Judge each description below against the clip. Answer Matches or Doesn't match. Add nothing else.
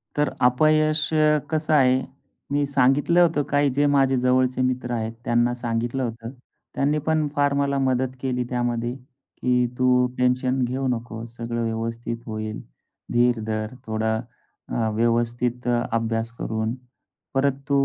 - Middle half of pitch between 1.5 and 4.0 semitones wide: Matches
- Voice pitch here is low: Matches